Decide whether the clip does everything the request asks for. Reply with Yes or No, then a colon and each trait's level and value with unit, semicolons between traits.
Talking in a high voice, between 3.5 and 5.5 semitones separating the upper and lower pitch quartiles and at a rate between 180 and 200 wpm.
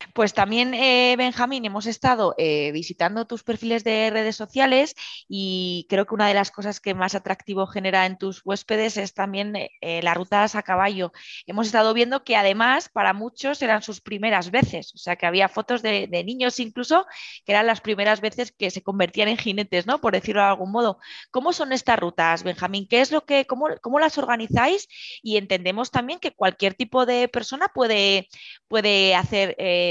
Yes: high, 215 Hz; average, 4.2 semitones; fast, 190 wpm